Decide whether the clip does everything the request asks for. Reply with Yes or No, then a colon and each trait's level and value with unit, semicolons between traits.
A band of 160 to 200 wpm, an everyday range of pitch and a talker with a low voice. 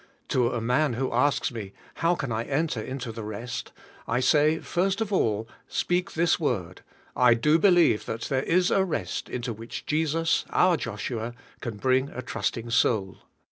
No: average, 170 wpm; wide, 6.0 semitones; low, 125 Hz